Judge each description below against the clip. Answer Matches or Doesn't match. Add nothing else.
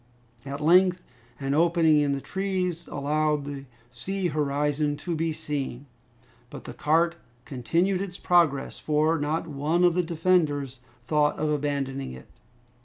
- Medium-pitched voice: Matches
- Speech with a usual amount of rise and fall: Matches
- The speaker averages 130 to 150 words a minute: Matches